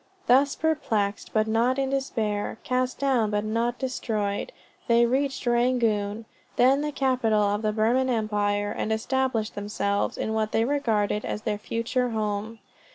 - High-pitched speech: Yes, high, 225 Hz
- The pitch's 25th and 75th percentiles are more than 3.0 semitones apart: Yes, average, 3.4 semitones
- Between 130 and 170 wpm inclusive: Yes, average, 150 wpm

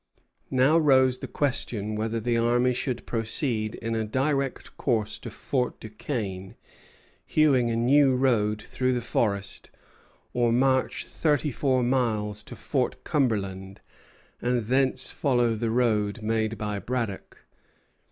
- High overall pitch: No, low, 120 Hz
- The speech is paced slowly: Yes, slow, 130 wpm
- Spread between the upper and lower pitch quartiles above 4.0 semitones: No, average, 3.2 semitones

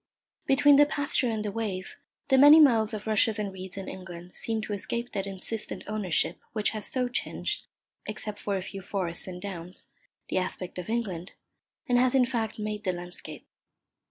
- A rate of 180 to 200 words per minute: Yes, average, 185 wpm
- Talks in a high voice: Yes, high, 210 Hz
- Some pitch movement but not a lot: Yes, average, 4.0 semitones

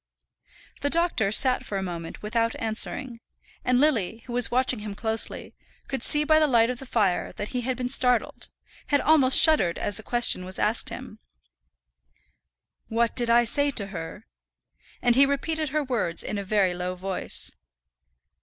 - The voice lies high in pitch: Yes, high, 235 Hz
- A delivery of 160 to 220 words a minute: Yes, average, 175 wpm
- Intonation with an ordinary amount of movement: Yes, average, 4.5 semitones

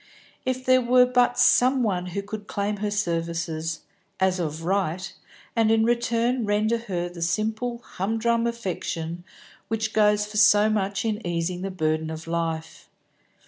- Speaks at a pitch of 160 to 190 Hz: No, high, 205 Hz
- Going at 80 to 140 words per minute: No, average, 155 wpm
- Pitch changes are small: No, average, 4.7 semitones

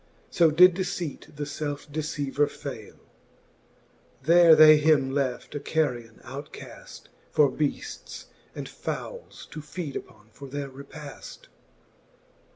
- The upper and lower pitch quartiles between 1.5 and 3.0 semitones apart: Yes, narrow, 2.4 semitones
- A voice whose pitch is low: No, medium, 145 Hz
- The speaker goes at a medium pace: No, slow, 115 wpm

